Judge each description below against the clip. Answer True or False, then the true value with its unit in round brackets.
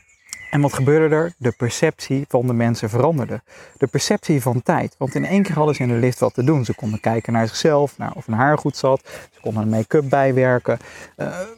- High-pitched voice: False (135 Hz)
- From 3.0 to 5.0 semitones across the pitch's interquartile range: True (4.2 semitones)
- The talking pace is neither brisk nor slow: False (225 wpm)